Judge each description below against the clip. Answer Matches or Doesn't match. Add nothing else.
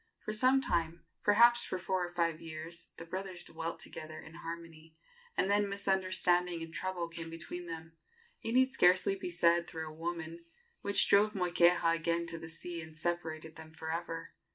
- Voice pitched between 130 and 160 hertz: Doesn't match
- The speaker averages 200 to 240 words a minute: Doesn't match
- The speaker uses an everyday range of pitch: Doesn't match